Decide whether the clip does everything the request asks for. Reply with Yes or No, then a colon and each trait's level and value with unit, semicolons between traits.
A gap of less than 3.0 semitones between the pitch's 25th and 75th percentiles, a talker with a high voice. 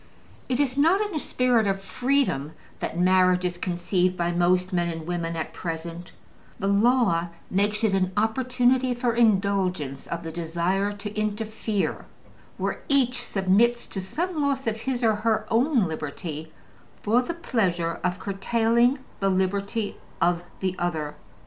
No: average, 5.3 semitones; high, 200 Hz